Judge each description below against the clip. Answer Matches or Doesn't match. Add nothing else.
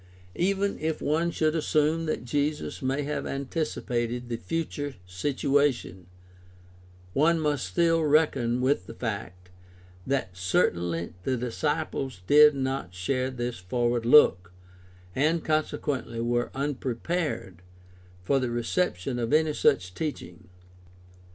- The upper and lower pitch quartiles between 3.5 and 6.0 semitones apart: Matches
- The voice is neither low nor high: Doesn't match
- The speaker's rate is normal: Doesn't match